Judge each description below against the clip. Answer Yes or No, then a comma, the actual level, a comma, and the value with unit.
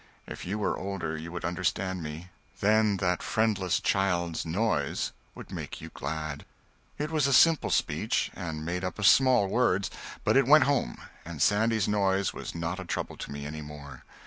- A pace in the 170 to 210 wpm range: Yes, average, 180 wpm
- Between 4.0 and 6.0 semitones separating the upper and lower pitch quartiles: Yes, average, 4.6 semitones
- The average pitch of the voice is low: Yes, very low, 95 Hz